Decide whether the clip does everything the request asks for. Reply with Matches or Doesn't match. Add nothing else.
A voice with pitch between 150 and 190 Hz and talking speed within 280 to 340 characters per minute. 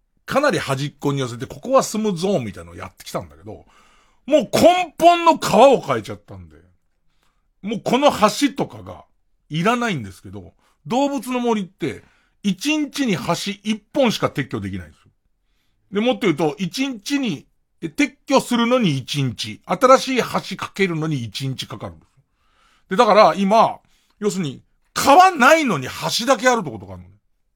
Matches